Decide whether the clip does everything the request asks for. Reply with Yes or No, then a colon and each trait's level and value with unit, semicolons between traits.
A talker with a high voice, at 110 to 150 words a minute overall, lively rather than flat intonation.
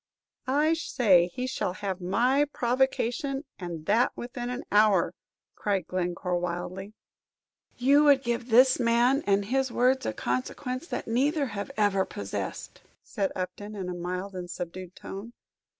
Yes: high, 210 Hz; average, 145 wpm; wide, 5.7 semitones